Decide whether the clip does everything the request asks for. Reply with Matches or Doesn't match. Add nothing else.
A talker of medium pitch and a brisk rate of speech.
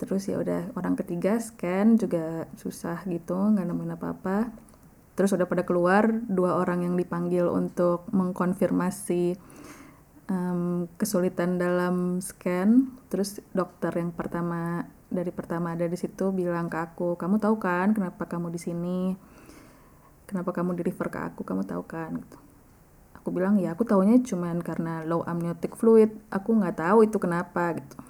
Matches